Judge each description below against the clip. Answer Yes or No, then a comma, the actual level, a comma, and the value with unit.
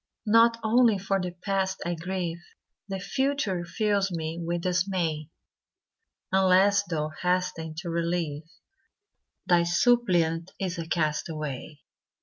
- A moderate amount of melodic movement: Yes, average, 3.0 semitones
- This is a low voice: No, medium, 180 Hz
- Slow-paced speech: Yes, slow, 100 wpm